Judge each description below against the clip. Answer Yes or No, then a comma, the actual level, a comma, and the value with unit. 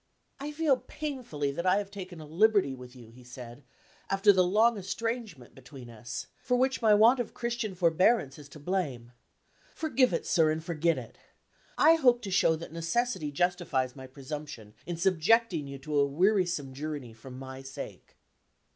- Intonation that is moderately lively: No, wide, 7.9 semitones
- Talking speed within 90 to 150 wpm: No, average, 175 wpm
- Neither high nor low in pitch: Yes, medium, 165 Hz